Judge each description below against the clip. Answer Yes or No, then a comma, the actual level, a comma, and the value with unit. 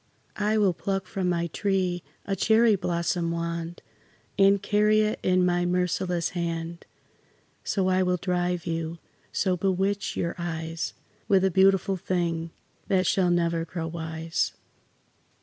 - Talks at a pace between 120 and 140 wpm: Yes, slow, 135 wpm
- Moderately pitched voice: Yes, medium, 180 Hz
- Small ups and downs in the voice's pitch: Yes, narrow, 2.3 semitones